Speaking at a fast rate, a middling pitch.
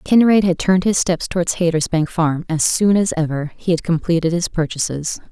No: average, 190 wpm; medium, 170 Hz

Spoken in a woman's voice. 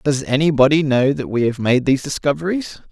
No: male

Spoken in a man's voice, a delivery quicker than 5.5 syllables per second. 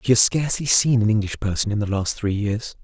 Yes: male; 6.0 syllables/s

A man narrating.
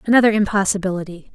No: female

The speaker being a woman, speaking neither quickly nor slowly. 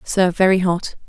Yes: female; average, 165 wpm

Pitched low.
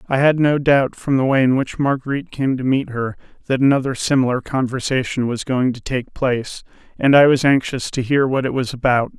Yes: low, 130 Hz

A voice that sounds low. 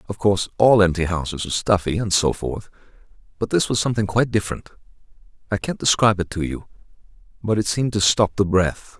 Yes: low, 100 Hz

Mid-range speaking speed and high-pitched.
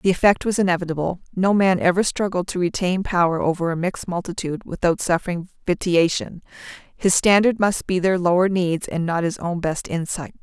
No: average, 180 wpm; medium, 180 Hz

